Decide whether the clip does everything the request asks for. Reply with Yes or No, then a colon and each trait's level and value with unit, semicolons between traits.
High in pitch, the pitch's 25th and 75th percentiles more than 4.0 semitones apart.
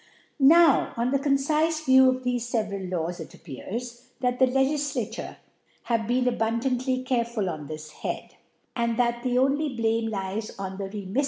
No: high, 240 Hz; average, 3.6 semitones